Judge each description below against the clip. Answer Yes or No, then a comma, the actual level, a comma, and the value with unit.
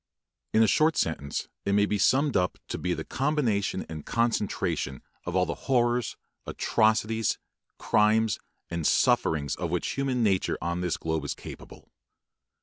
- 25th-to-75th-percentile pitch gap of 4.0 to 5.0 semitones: No, wide, 5.5 semitones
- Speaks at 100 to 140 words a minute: No, average, 150 wpm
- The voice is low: Yes, low, 105 Hz